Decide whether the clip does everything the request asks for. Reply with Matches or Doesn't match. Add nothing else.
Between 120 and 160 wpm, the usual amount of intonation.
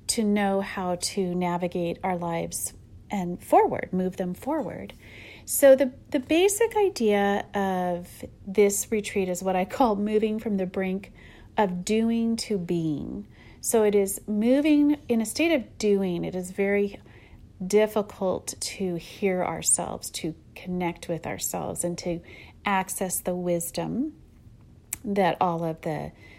Matches